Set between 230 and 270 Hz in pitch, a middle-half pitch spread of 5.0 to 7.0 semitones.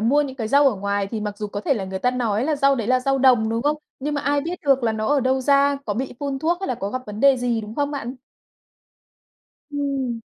No: very high, 255 Hz; average, 4.3 semitones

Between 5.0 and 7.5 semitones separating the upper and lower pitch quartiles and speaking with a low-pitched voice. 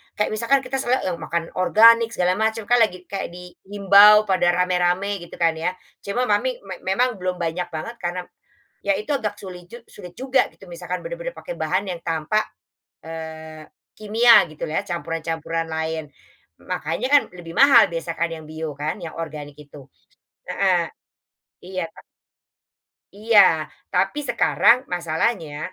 No: wide, 5.5 semitones; medium, 185 Hz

